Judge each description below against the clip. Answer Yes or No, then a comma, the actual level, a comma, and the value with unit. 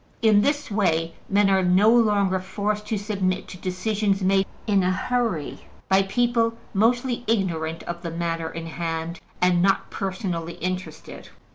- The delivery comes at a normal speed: Yes, average, 150 wpm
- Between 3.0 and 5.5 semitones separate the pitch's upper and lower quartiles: Yes, average, 3.6 semitones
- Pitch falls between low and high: No, high, 195 Hz